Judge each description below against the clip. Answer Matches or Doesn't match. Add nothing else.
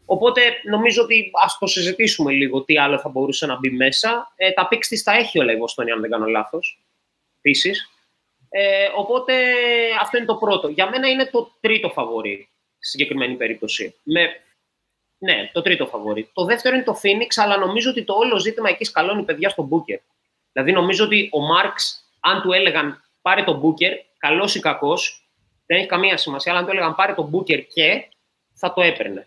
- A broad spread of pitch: Matches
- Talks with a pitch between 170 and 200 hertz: Matches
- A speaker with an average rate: Doesn't match